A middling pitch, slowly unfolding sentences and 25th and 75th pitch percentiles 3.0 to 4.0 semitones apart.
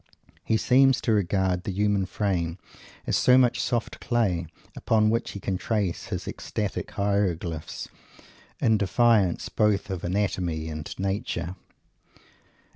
No: low, 100 Hz; slow, 125 wpm; average, 3.7 semitones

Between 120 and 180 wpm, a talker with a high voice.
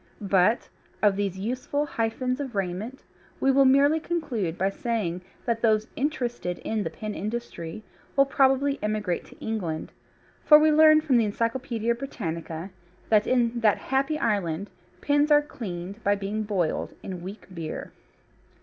Yes: average, 150 wpm; high, 225 Hz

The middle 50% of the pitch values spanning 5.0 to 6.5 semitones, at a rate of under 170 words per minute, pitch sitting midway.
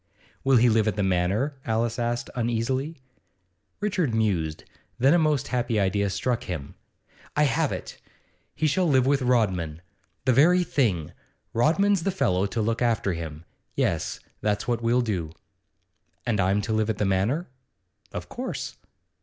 No: average, 5.3 semitones; average, 155 wpm; low, 115 Hz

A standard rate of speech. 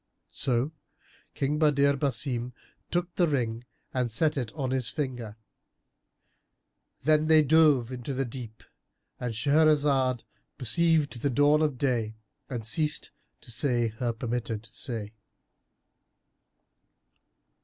No: slow, 110 wpm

